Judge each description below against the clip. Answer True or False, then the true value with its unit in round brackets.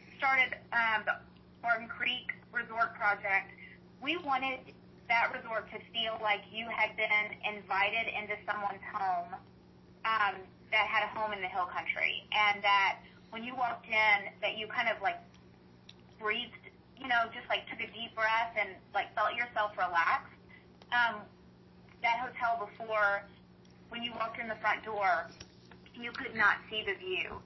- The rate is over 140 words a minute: True (155 wpm)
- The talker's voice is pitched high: True (215 Hz)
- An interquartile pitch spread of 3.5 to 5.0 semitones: False (2.7 semitones)